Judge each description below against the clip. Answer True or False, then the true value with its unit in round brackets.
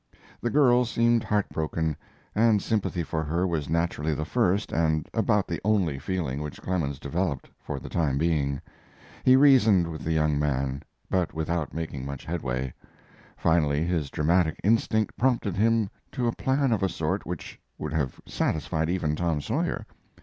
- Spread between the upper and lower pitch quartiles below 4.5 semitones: False (5.5 semitones)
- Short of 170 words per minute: True (160 wpm)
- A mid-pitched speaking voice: False (85 Hz)